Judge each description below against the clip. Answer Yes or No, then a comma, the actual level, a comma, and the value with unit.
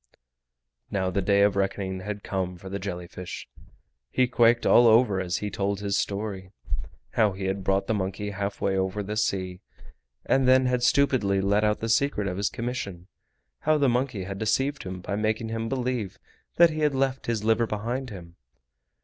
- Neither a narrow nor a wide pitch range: Yes, average, 3.8 semitones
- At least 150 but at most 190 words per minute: Yes, average, 185 wpm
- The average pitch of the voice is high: No, low, 105 Hz